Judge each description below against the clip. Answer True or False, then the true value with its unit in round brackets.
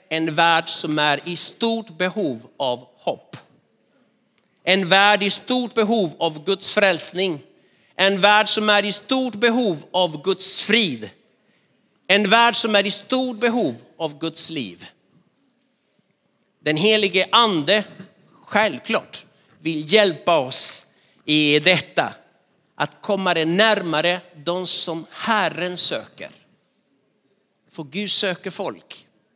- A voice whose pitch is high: True (195 Hz)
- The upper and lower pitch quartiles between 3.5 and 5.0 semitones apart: True (3.9 semitones)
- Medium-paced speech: False (120 wpm)